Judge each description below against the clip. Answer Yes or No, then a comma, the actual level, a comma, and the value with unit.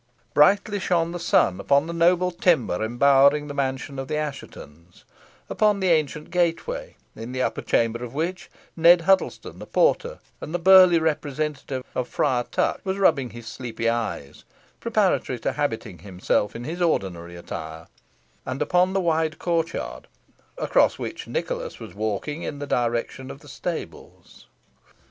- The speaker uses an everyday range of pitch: No, wide, 6.5 semitones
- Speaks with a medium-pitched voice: Yes, medium, 150 Hz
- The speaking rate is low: No, average, 155 wpm